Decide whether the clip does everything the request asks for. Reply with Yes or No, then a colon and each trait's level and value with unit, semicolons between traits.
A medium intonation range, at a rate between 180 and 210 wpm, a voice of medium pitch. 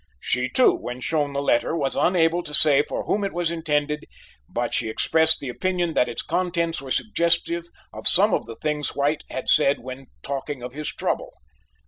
Yes: average, 3.7 semitones; average, 190 wpm; medium, 150 Hz